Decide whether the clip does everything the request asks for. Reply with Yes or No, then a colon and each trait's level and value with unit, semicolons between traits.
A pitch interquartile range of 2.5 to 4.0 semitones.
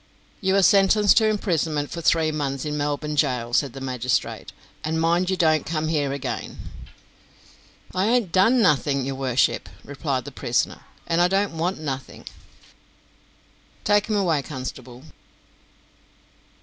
No: wide, 5.4 semitones